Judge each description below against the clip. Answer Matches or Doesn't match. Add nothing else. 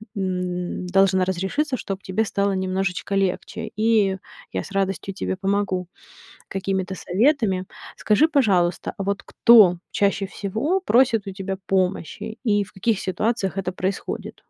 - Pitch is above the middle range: Matches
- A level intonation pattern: Matches